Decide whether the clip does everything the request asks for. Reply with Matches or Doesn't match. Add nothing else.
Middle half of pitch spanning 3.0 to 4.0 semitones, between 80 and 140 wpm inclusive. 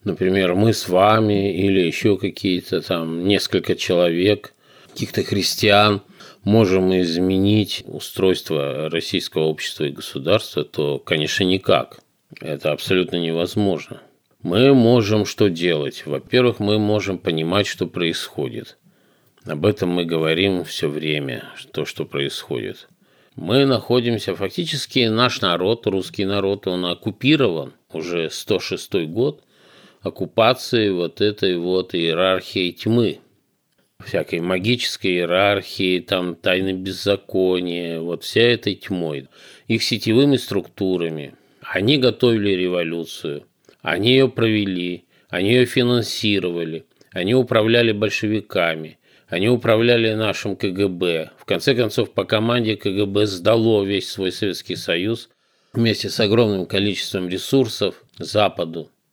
Matches